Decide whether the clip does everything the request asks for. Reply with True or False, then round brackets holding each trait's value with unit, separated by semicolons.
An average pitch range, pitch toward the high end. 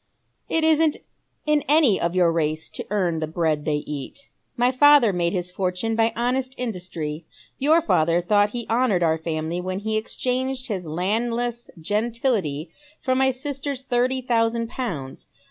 False (7.0 semitones; 220 Hz)